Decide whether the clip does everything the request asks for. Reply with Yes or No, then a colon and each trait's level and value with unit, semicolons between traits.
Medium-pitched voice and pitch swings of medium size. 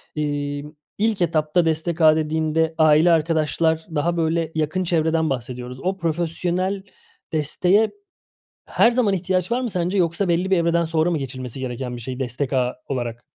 Yes: medium, 160 Hz; average, 3.3 semitones